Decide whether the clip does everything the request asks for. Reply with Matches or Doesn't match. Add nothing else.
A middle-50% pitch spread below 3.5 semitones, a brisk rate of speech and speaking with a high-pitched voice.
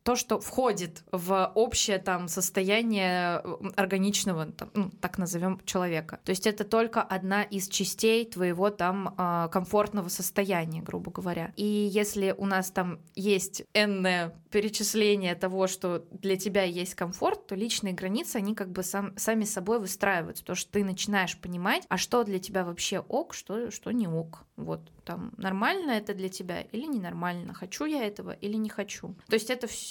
Matches